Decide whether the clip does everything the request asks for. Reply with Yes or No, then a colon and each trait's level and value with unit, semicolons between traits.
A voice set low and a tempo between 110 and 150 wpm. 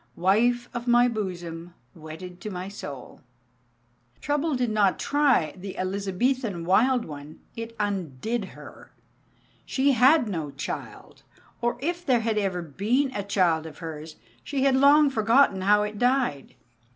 No: high, 210 Hz; average, 140 wpm